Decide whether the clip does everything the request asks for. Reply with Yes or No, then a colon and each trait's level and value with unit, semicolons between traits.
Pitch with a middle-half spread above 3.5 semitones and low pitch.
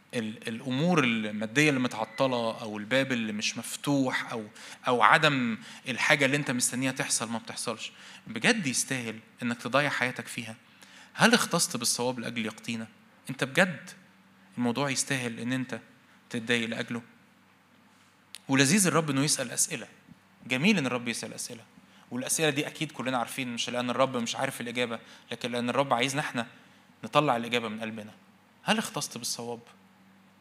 No: average, 2.7 semitones; low, 120 Hz